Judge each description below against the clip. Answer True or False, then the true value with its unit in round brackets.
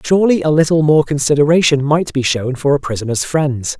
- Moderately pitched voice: True (145 Hz)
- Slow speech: False (190 wpm)